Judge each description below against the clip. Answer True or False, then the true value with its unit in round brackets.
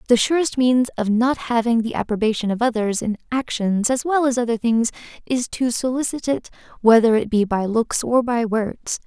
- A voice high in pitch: True (235 Hz)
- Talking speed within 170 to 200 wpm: True (190 wpm)